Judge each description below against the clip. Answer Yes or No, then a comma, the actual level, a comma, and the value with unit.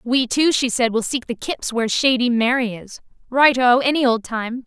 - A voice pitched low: No, high, 245 Hz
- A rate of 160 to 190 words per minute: No, fast, 205 wpm